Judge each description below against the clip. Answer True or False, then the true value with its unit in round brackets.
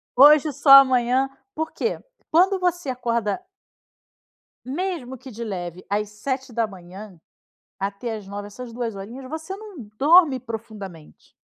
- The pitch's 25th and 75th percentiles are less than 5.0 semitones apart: False (5.6 semitones)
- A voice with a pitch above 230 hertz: True (245 Hz)